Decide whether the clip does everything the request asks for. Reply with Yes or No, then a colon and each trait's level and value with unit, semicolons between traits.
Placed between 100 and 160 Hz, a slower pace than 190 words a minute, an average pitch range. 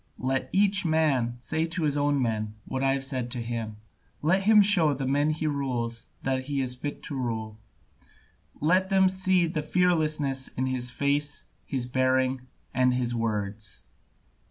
Yes: low, 135 Hz; average, 165 wpm; average, 4.1 semitones